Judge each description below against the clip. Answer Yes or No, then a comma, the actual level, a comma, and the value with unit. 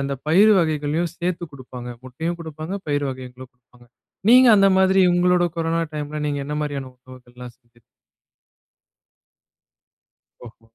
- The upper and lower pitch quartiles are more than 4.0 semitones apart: Yes, average, 4.9 semitones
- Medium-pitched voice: Yes, medium, 145 Hz